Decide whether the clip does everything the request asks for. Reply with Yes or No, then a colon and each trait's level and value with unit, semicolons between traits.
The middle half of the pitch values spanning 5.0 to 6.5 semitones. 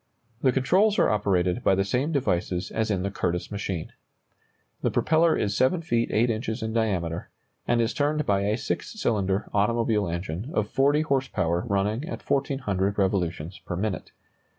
Yes: average, 5.3 semitones